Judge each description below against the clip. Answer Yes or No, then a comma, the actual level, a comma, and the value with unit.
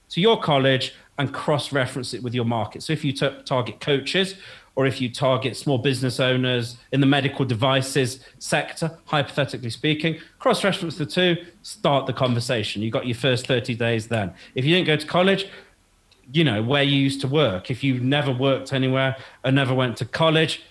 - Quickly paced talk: No, average, 195 wpm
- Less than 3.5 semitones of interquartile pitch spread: Yes, average, 3.0 semitones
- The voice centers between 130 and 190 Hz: Yes, low, 135 Hz